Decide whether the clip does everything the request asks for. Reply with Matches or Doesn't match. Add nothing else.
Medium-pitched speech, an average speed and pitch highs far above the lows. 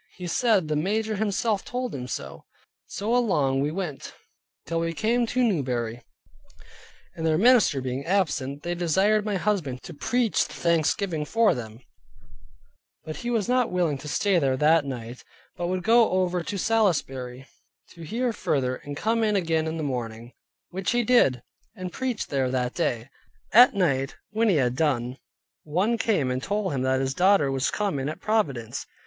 Matches